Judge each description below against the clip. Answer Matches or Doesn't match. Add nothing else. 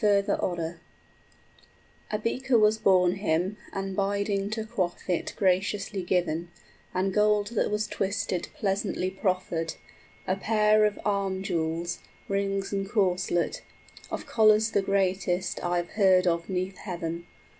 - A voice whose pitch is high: Matches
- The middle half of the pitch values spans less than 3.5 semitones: Matches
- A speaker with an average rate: Doesn't match